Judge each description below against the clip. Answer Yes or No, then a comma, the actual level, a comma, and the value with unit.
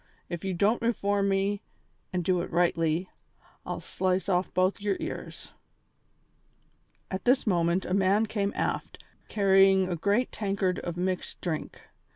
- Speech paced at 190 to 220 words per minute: No, average, 145 wpm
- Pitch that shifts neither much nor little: No, narrow, 2.0 semitones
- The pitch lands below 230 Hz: Yes, high, 190 Hz